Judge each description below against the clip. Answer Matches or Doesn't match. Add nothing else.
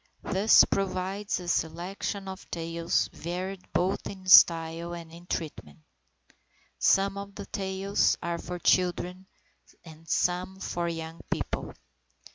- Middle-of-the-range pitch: Matches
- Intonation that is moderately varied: Doesn't match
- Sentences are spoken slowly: Matches